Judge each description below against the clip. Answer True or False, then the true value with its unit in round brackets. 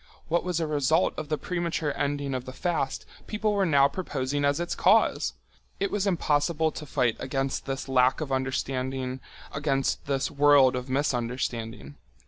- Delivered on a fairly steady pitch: False (3.2 semitones)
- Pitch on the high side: False (140 Hz)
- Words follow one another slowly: False (160 wpm)